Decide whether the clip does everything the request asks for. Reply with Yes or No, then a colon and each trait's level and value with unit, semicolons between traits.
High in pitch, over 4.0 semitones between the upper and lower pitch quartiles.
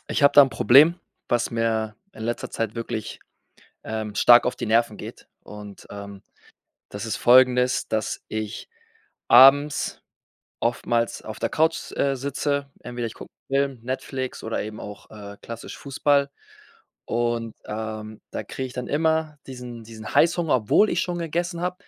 No: low, 120 Hz; average, 4.4 semitones